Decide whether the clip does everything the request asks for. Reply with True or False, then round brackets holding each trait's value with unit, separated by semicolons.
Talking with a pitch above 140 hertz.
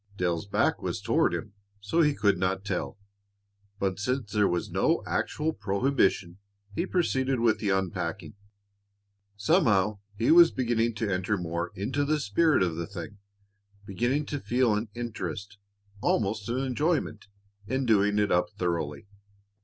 False (105 Hz)